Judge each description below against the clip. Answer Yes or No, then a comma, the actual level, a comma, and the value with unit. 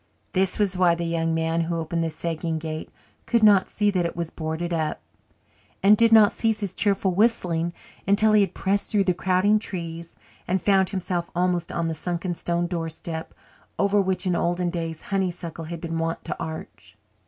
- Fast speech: No, average, 190 wpm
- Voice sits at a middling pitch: Yes, medium, 175 Hz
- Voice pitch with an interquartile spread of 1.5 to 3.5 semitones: Yes, average, 2.8 semitones